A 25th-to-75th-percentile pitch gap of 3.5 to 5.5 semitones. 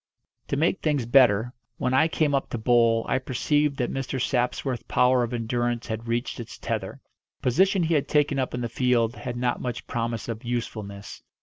No: narrow, 2.6 semitones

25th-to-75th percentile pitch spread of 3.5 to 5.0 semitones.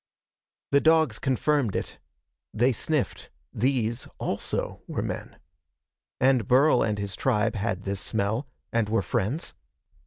Yes: average, 4.3 semitones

